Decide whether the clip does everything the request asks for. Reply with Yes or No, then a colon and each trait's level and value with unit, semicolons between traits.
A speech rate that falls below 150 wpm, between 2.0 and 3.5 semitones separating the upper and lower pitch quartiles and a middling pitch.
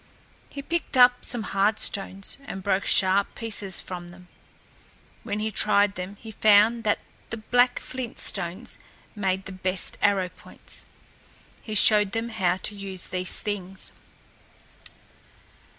No: slow, 135 wpm; average, 2.7 semitones; high, 205 Hz